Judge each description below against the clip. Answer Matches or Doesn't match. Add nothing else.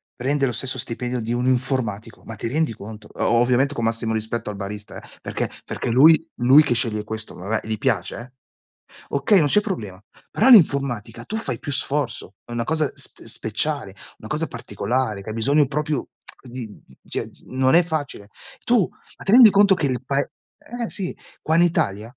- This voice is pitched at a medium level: Doesn't match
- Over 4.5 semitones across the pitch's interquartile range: Matches